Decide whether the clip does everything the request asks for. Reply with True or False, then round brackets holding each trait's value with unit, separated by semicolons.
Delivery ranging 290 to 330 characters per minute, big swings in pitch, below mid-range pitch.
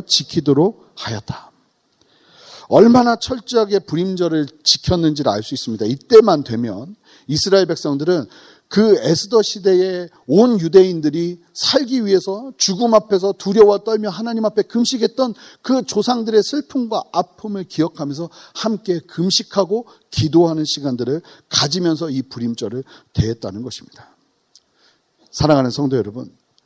False (305 characters per minute; 6.0 semitones; 180 Hz)